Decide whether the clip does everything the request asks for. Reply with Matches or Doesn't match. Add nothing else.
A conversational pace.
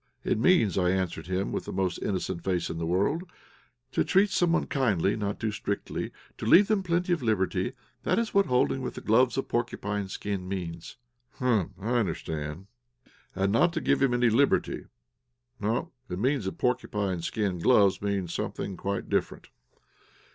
Matches